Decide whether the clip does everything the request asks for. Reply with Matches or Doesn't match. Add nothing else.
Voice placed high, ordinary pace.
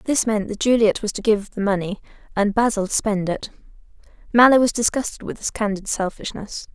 Matches